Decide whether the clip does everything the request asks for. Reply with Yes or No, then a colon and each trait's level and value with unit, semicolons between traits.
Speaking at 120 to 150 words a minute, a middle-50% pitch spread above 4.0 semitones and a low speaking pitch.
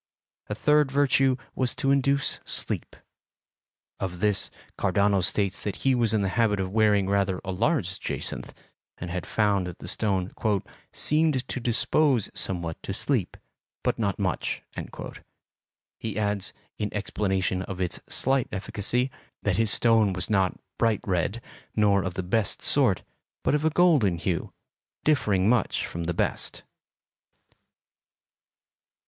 Yes: average, 140 wpm; average, 4.6 semitones; low, 105 Hz